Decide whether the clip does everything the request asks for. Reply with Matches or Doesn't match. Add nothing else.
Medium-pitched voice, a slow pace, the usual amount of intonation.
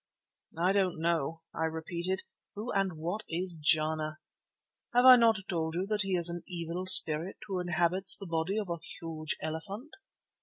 Doesn't match